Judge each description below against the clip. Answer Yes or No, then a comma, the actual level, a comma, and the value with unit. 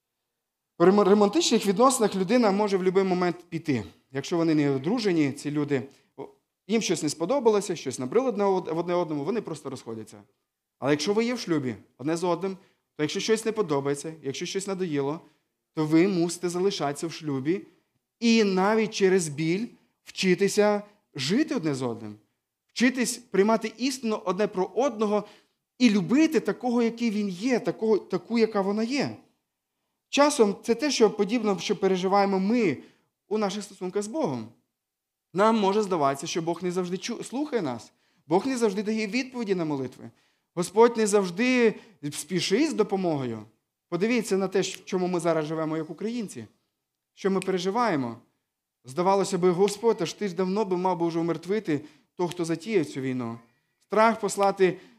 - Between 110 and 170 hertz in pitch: No, high, 190 Hz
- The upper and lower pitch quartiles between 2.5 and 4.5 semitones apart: No, average, 5.2 semitones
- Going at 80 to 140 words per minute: No, fast, 155 wpm